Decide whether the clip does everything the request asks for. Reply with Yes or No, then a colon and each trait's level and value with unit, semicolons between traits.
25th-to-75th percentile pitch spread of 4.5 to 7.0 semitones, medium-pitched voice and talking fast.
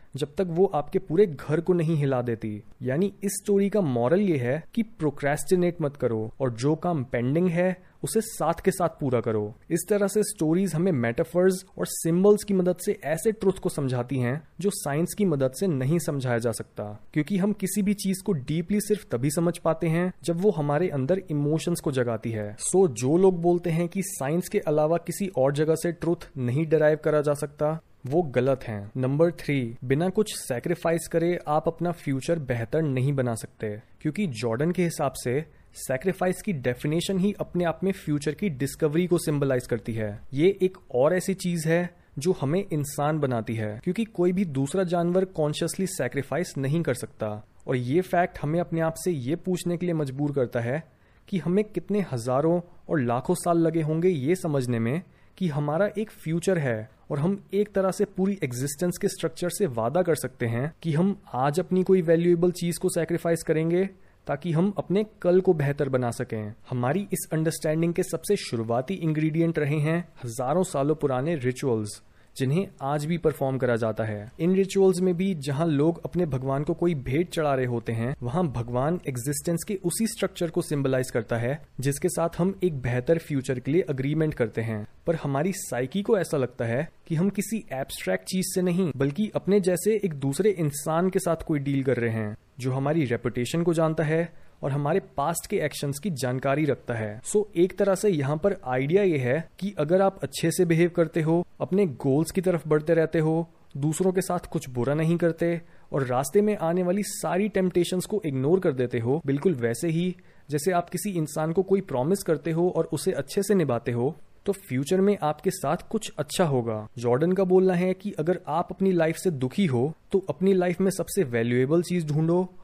Yes: average, 5.1 semitones; medium, 165 Hz; fast, 200 wpm